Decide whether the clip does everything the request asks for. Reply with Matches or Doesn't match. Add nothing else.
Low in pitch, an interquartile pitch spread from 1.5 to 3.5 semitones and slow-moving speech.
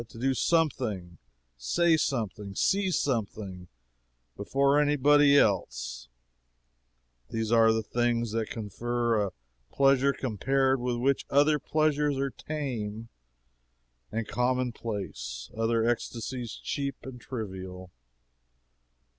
Doesn't match